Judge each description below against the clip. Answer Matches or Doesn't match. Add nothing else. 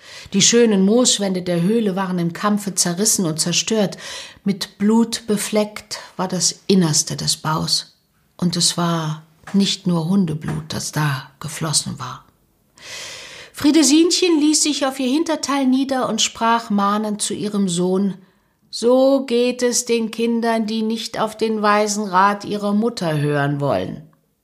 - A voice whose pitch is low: Doesn't match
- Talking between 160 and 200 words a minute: Doesn't match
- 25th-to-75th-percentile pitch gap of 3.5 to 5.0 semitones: Matches